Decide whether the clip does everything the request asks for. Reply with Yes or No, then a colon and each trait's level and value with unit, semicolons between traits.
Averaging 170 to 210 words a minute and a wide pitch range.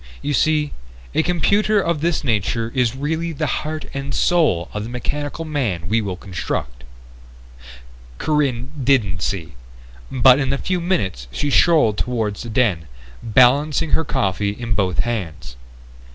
No: average, 145 wpm; wide, 6.7 semitones